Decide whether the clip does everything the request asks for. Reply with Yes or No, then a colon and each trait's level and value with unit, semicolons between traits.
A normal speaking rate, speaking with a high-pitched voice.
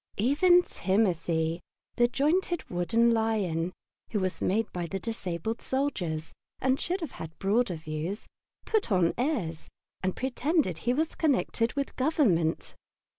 No: slow, 130 wpm; high, 220 Hz